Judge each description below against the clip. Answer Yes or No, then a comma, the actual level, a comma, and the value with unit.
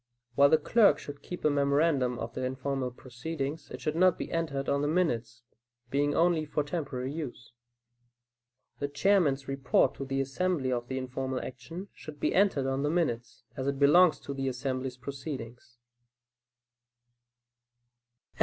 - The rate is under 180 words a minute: Yes, average, 155 wpm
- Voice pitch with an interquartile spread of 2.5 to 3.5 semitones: Yes, average, 3.2 semitones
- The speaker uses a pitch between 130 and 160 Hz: Yes, medium, 140 Hz